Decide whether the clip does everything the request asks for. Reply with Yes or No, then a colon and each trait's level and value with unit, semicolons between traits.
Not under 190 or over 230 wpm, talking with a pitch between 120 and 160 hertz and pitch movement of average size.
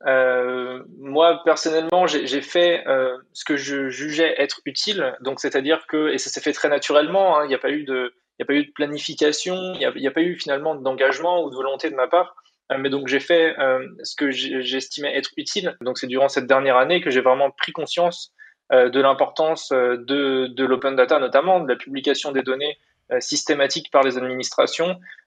Yes: average, 215 wpm; medium, 140 Hz; average, 3.6 semitones